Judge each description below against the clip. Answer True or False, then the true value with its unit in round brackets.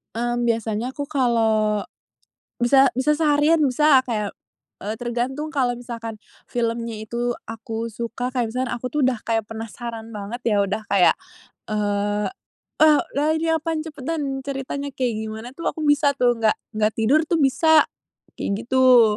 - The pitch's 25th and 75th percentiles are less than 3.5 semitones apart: False (3.8 semitones)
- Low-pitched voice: False (240 Hz)